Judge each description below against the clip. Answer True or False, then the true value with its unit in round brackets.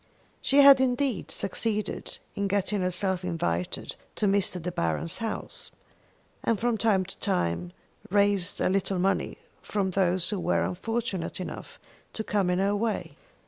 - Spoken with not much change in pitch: False (3.0 semitones)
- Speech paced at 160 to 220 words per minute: False (145 wpm)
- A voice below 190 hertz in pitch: False (195 Hz)